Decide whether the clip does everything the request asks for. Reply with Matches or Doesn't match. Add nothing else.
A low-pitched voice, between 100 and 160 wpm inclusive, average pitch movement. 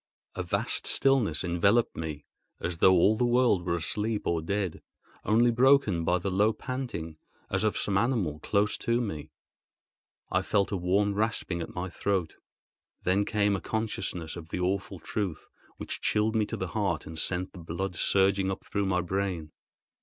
Doesn't match